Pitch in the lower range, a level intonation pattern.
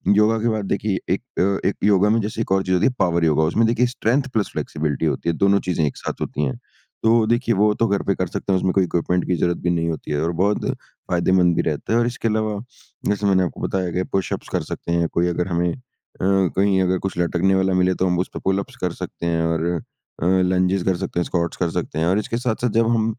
No: very low, 95 Hz; average, 3.4 semitones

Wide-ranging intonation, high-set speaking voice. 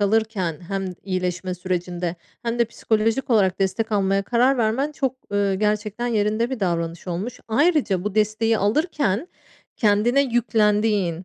No: average, 3.6 semitones; high, 210 Hz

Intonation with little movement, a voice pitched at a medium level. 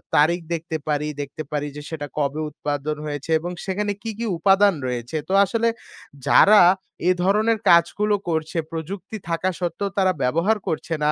No: average, 4.9 semitones; medium, 170 Hz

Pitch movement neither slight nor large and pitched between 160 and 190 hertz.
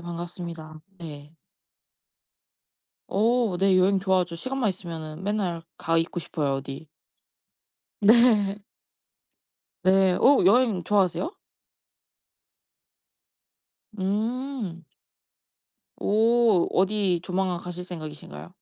Yes: average, 3.7 semitones; medium, 185 Hz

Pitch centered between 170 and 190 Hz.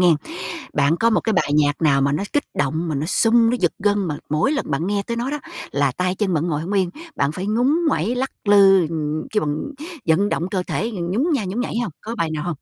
Yes: medium, 185 Hz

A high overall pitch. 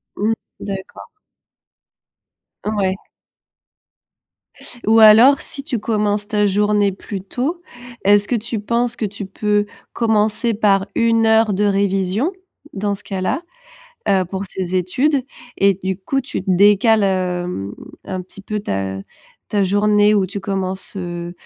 Yes: high, 205 Hz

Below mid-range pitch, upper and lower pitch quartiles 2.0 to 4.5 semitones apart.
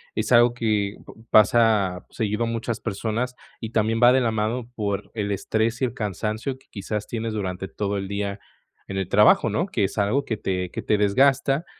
Yes: low, 110 Hz; narrow, 2.6 semitones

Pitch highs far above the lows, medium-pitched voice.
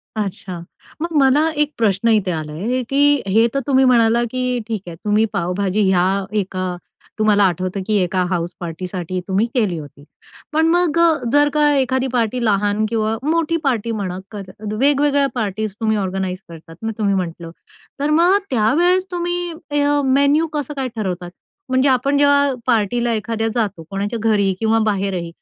No: wide, 6.4 semitones; high, 220 Hz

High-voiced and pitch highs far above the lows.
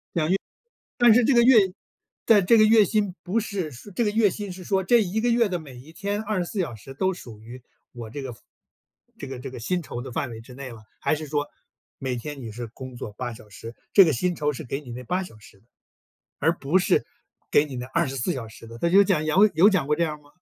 No: medium, 155 Hz; wide, 7.6 semitones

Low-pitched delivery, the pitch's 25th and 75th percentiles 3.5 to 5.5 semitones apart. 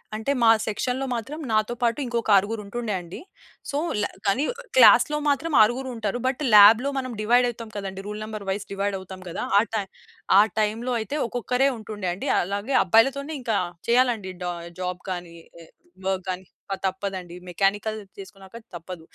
No: high, 215 Hz; average, 4.0 semitones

